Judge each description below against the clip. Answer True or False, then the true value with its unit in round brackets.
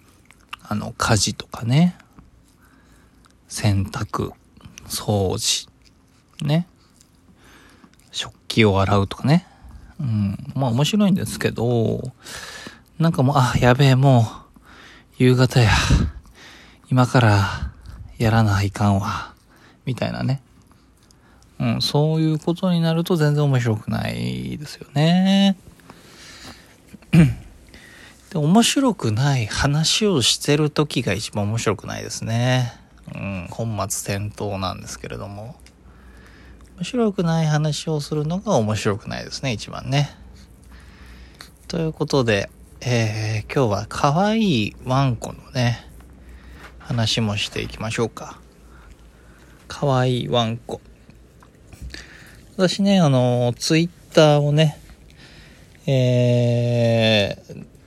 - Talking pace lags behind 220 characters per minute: True (200 characters per minute)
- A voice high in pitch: False (120 Hz)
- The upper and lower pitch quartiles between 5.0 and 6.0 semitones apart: False (6.8 semitones)